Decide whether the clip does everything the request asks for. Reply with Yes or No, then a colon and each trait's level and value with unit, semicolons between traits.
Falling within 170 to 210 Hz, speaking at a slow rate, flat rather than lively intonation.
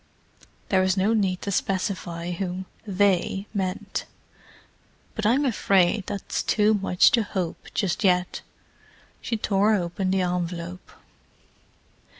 Yes: high, 190 Hz; slow, 120 wpm; narrow, 2.3 semitones